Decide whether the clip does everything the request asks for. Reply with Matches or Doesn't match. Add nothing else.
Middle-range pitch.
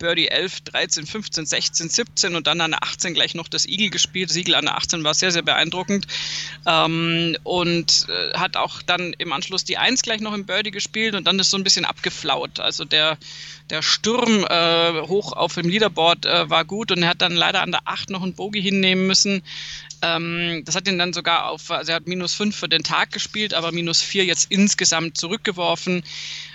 Matches